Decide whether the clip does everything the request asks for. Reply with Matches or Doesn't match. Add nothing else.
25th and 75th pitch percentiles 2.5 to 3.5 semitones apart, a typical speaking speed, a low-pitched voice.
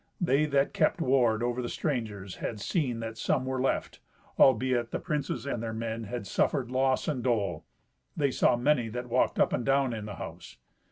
Matches